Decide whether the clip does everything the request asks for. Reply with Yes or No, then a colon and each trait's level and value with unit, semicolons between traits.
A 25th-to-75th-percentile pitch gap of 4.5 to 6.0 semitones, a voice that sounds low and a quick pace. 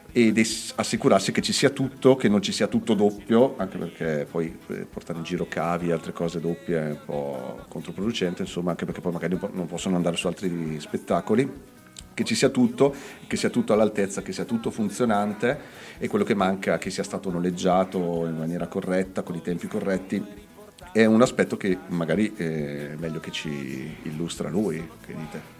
Yes: average, 5.1 semitones; very low, 90 Hz; fast, 185 wpm